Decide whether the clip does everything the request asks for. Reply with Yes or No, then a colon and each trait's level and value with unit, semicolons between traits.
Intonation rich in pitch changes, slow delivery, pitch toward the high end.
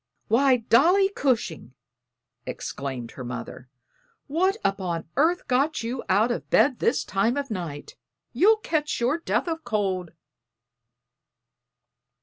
Yes: wide, 8.6 semitones; slow, 120 wpm; high, 240 Hz